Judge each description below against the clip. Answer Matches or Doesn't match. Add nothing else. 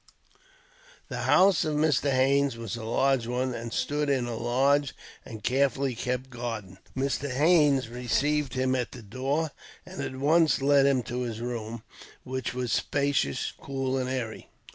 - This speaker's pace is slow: Doesn't match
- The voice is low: Matches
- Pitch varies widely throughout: Doesn't match